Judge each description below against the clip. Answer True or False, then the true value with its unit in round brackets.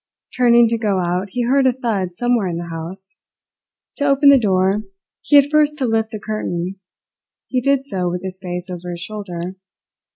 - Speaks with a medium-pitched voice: False (205 Hz)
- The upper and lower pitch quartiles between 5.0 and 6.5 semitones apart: True (5.5 semitones)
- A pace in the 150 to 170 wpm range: False (190 wpm)